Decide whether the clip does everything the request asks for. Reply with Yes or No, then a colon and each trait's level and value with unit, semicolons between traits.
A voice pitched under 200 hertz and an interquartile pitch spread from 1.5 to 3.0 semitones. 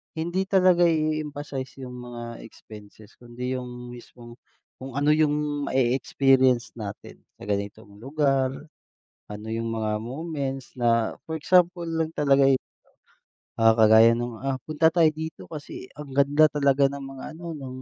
No: low, 135 Hz; average, 4.2 semitones